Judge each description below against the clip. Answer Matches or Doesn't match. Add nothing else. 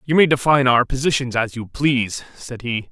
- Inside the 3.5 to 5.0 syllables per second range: Doesn't match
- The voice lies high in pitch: Doesn't match